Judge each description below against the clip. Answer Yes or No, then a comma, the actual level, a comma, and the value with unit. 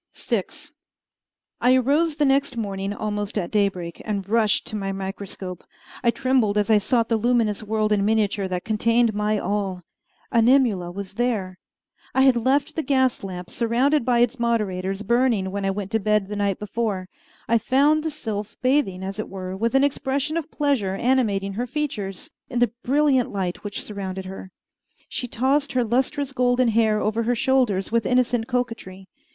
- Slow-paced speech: No, average, 175 wpm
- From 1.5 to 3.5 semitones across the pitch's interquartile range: No, average, 4.4 semitones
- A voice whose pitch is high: Yes, high, 220 Hz